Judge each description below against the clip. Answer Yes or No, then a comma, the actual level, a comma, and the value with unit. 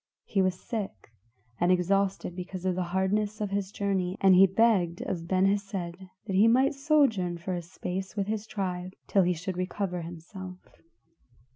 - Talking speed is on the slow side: No, average, 170 wpm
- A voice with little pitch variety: Yes, narrow, 2.1 semitones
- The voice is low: No, high, 190 Hz